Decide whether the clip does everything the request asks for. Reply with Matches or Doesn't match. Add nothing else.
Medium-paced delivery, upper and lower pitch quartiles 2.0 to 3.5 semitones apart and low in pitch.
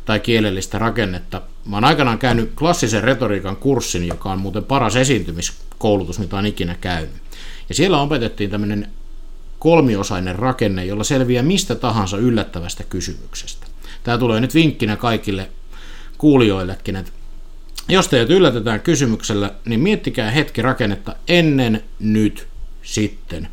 Doesn't match